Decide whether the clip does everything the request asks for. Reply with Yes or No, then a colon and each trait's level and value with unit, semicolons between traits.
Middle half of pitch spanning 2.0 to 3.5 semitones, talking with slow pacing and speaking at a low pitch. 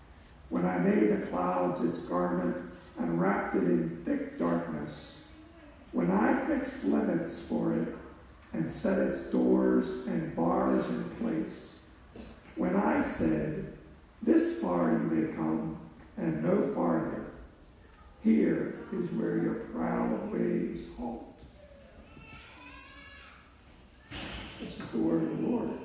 No: average, 4.4 semitones; slow, 120 wpm; very low, 80 Hz